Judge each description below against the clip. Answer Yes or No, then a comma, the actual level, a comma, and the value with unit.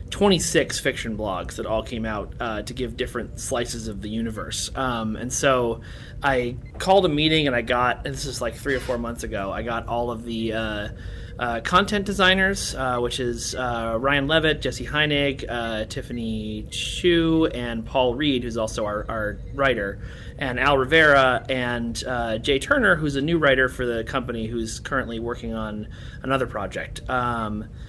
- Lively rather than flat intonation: No, average, 3.1 semitones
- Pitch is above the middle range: No, low, 120 Hz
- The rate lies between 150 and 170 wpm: No, average, 180 wpm